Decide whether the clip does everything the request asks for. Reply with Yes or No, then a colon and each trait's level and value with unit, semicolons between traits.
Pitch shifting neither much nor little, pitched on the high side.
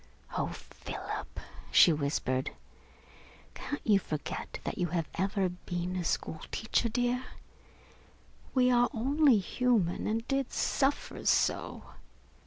No: wide, 6.1 semitones; high, 210 Hz